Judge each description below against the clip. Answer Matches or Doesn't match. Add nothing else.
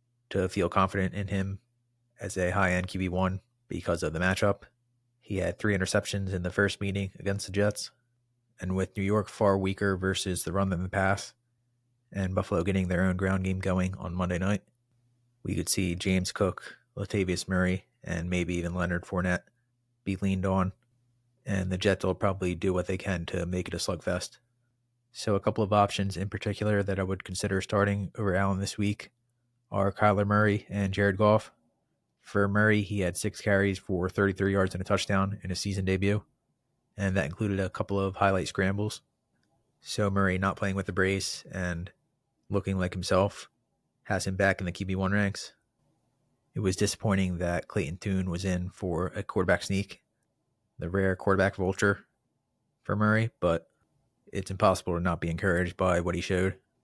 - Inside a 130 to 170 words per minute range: Doesn't match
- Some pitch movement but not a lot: Doesn't match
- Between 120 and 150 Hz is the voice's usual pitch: Doesn't match